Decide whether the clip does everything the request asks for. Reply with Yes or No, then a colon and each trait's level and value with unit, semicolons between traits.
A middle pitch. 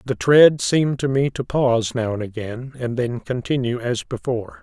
No: low, 125 Hz